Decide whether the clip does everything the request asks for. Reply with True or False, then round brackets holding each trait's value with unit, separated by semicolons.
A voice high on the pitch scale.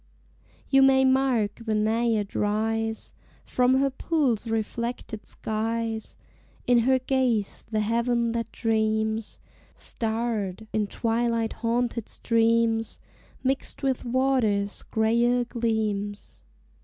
True (230 Hz)